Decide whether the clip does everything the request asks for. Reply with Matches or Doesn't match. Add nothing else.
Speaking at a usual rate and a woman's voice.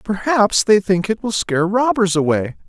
Doesn't match